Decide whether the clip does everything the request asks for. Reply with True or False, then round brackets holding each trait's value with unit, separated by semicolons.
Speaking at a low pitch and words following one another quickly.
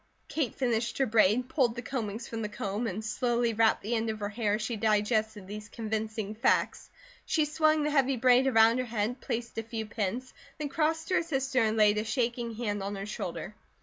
False (230 Hz; 215 wpm)